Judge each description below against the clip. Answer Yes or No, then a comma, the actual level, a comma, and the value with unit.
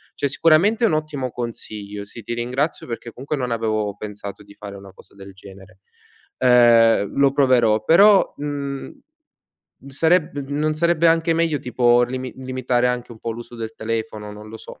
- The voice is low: Yes, low, 120 Hz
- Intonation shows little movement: No, average, 4.9 semitones